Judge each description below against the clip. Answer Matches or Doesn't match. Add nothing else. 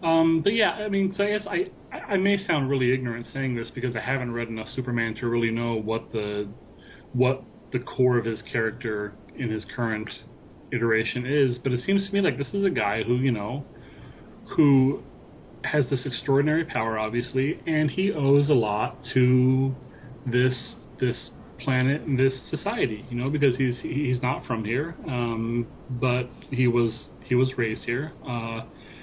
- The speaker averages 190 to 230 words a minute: Doesn't match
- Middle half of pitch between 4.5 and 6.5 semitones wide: Doesn't match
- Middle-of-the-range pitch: Doesn't match